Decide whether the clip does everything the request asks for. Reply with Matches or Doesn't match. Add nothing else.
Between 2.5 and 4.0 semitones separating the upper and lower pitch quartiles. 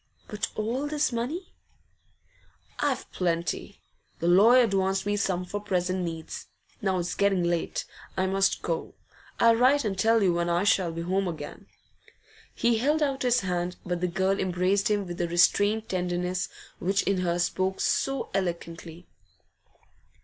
Matches